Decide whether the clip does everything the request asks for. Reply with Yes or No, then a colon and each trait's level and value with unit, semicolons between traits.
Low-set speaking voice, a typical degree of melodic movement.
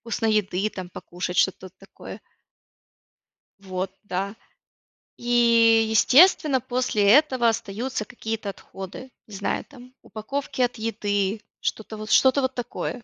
No: high, 220 Hz; average, 3.8 semitones